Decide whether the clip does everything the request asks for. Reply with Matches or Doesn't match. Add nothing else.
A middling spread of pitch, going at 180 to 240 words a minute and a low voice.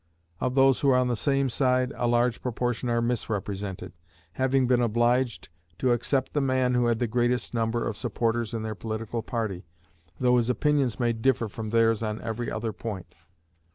Doesn't match